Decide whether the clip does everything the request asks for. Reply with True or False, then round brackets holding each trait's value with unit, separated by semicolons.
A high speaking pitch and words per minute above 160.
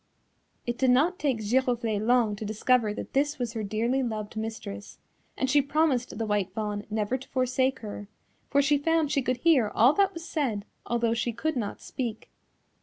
True (245 Hz; 185 wpm)